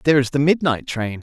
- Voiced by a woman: No, male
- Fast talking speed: Yes, fast, 245 wpm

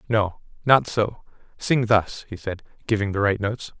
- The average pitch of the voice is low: Yes, low, 105 Hz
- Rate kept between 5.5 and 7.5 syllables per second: No, 4.7 syllables/s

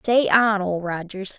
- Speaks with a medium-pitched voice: No, high, 200 Hz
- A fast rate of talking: No, average, 175 wpm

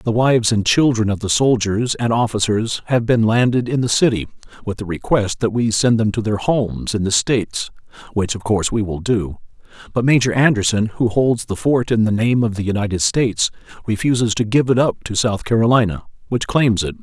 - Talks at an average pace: No, fast, 210 wpm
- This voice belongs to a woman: No, male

